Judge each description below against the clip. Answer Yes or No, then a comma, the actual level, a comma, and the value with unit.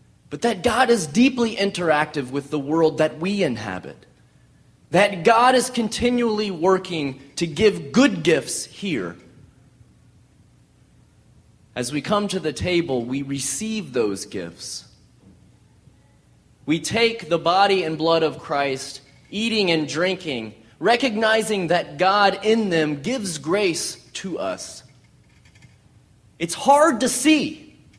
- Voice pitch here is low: No, medium, 170 Hz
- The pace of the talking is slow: Yes, slow, 120 wpm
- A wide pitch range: Yes, wide, 7.7 semitones